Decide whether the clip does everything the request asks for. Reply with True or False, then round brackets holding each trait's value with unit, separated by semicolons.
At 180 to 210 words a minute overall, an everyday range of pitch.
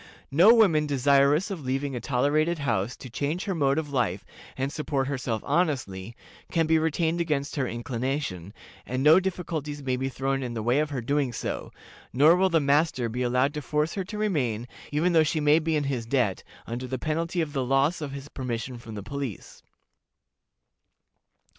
True (190 wpm; 3.7 semitones)